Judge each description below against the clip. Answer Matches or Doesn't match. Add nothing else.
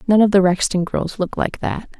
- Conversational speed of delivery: Doesn't match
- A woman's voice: Matches